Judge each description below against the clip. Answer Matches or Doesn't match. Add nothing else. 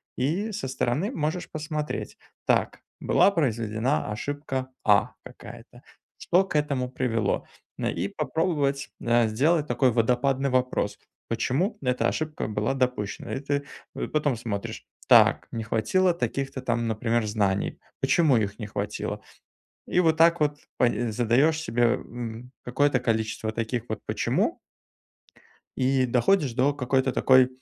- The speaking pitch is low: Matches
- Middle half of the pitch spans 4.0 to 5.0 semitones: Matches